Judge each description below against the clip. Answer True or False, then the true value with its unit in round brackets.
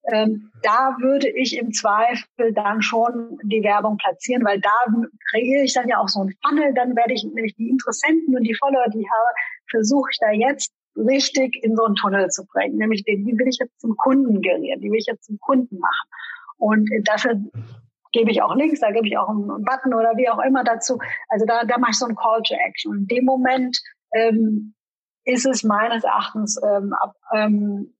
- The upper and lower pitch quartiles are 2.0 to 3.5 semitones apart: True (3.2 semitones)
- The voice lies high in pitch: True (230 Hz)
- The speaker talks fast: True (210 wpm)